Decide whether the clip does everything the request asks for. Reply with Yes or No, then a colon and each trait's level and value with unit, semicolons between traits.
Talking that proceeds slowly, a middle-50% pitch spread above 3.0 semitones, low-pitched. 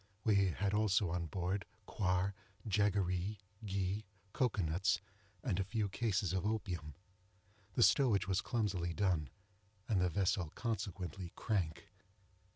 No: slow, 125 wpm; narrow, 2.6 semitones; very low, 95 Hz